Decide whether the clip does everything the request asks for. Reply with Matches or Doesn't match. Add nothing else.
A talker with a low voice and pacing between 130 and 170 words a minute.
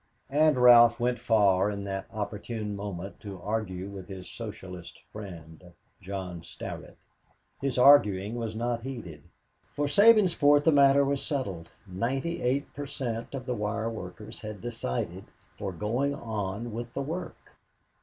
Matches